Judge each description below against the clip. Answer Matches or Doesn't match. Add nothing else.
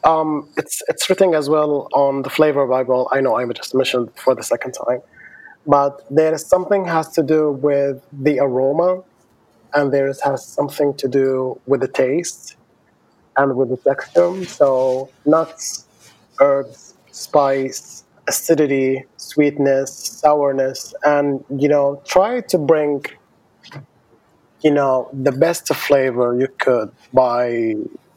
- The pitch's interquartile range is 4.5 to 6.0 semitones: Doesn't match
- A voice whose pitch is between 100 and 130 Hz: Doesn't match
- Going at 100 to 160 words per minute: Matches